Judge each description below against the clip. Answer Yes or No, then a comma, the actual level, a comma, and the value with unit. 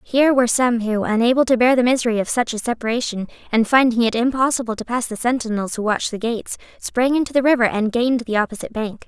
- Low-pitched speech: No, high, 235 Hz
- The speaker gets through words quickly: Yes, fast, 225 wpm